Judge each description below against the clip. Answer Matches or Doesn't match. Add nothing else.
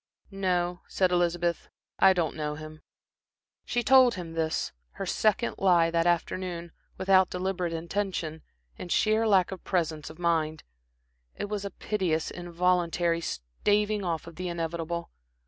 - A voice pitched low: Doesn't match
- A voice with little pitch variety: Matches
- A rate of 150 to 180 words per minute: Doesn't match